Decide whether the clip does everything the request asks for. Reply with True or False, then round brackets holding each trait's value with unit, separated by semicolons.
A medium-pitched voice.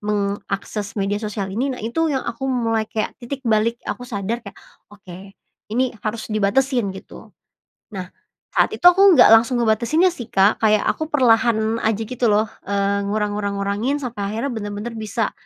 False (220 Hz)